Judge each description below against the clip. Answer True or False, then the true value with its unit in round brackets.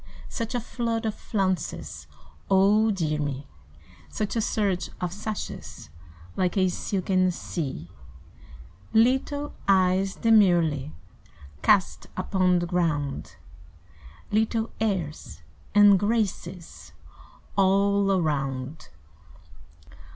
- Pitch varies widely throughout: False (3.7 semitones)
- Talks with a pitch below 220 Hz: True (190 Hz)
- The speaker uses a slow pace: True (90 wpm)